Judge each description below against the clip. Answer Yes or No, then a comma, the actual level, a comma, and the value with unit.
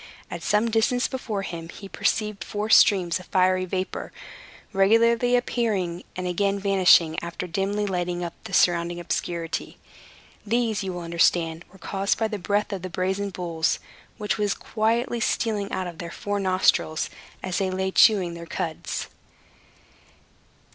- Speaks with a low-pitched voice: No, high, 190 Hz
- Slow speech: No, average, 150 wpm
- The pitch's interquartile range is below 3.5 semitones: Yes, average, 3.1 semitones